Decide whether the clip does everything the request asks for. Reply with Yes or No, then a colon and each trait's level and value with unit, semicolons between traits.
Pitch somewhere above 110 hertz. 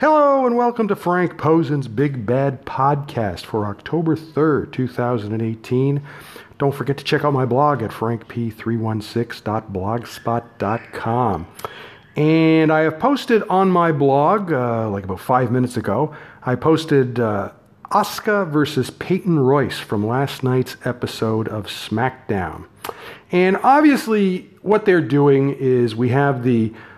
Yes: low, 135 Hz